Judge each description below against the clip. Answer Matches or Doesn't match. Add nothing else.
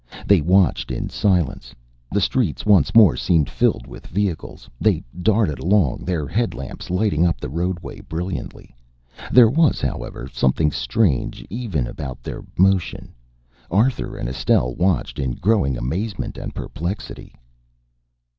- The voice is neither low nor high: Doesn't match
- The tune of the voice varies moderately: Doesn't match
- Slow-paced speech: Matches